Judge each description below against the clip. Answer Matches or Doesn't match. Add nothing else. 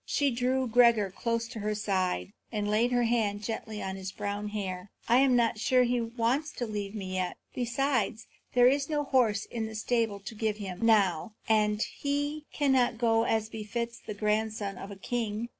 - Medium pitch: Doesn't match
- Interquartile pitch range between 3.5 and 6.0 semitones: Doesn't match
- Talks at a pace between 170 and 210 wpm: Matches